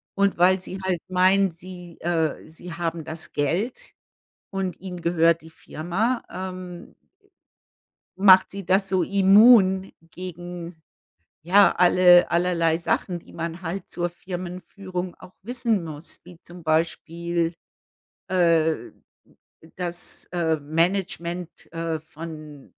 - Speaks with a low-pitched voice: No, medium, 175 Hz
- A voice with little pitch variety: Yes, narrow, 2.1 semitones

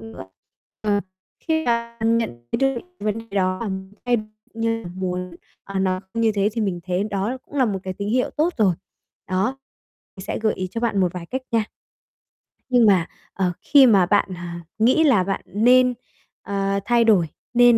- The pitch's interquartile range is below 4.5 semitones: Yes, average, 3.8 semitones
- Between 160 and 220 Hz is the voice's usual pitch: Yes, high, 205 Hz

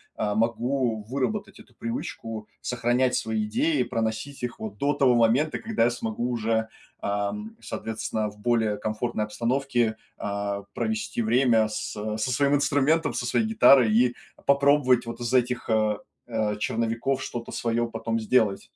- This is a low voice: Yes, low, 115 Hz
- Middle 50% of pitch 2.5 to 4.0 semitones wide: Yes, average, 2.9 semitones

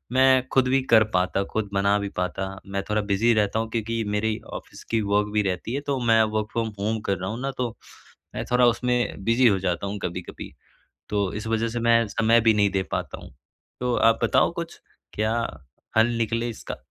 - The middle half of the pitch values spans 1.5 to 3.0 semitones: Yes, narrow, 2.5 semitones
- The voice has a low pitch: Yes, low, 110 Hz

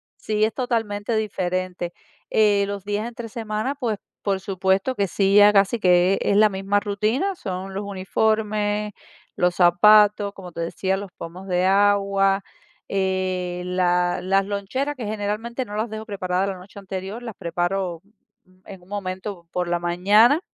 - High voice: Yes, high, 200 Hz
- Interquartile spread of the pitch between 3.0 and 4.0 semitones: No, narrow, 2.4 semitones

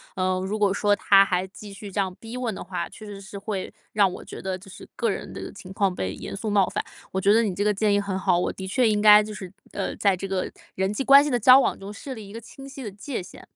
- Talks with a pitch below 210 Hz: Yes, high, 200 Hz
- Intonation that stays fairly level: Yes, narrow, 2.2 semitones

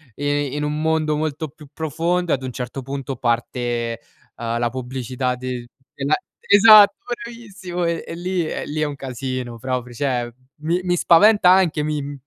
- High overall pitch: No, medium, 145 Hz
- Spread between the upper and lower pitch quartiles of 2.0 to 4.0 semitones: No, average, 4.7 semitones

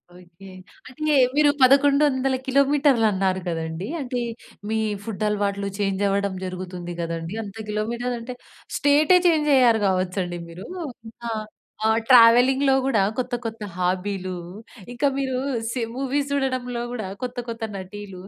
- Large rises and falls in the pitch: Yes, wide, 5.8 semitones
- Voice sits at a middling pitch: No, high, 225 Hz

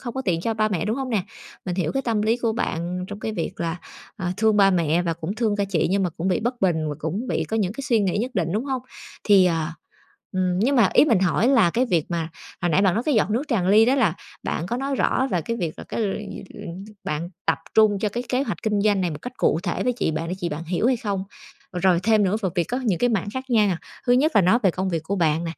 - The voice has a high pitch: Yes, high, 200 Hz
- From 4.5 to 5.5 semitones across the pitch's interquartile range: Yes, average, 4.8 semitones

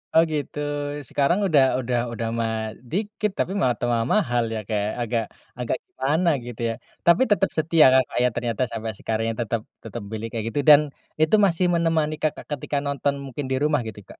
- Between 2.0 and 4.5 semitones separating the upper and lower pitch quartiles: No, wide, 5.4 semitones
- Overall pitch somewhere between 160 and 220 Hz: No, low, 135 Hz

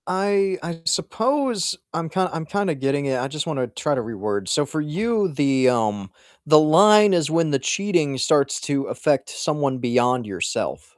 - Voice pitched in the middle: Yes, medium, 150 Hz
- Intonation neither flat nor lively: No, wide, 5.8 semitones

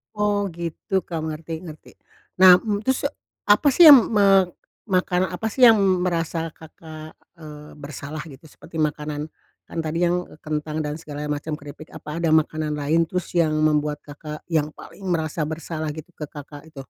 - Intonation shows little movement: Yes, narrow, 2.2 semitones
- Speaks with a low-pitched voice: No, medium, 155 Hz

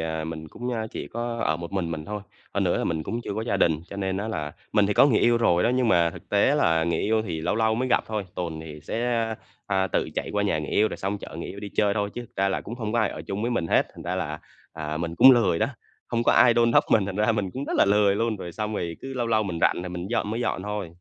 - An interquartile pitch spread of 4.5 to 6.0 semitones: Yes, average, 4.8 semitones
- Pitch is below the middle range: Yes, low, 100 Hz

